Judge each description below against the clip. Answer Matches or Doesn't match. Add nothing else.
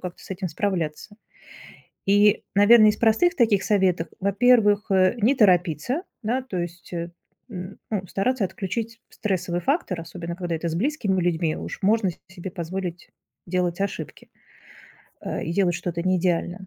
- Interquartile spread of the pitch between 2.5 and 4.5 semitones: Matches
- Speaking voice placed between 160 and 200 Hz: Matches